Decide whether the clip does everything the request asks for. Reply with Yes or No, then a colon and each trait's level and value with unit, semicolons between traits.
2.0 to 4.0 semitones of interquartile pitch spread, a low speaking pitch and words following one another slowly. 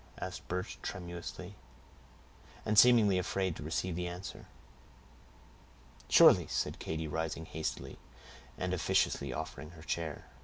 Yes: narrow, 2.6 semitones; very low, 85 Hz; slow, 115 wpm